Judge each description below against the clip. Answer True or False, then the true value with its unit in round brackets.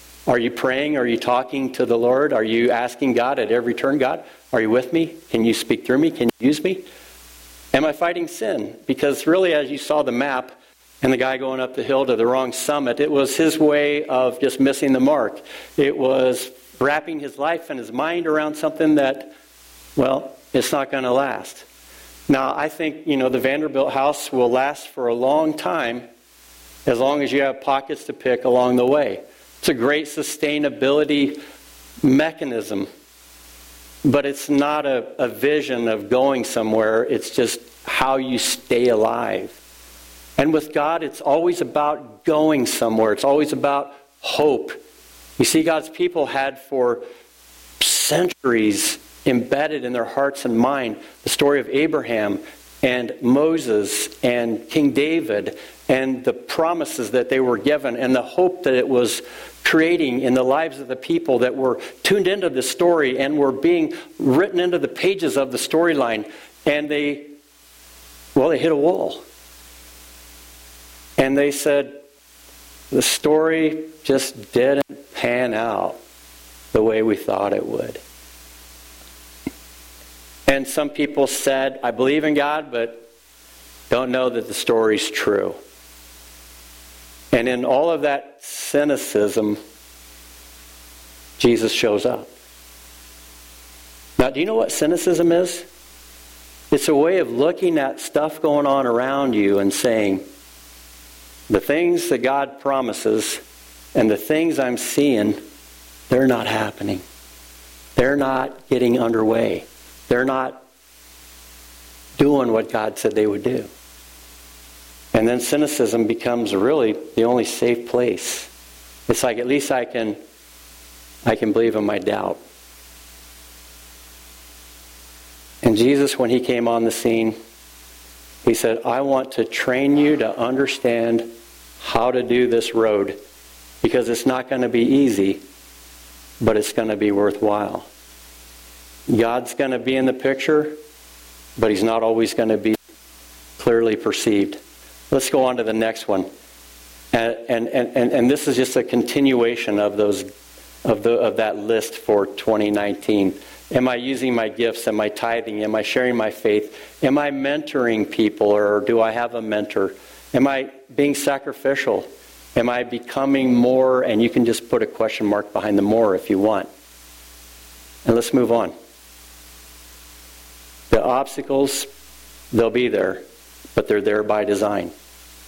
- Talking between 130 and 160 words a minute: True (150 wpm)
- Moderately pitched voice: False (120 Hz)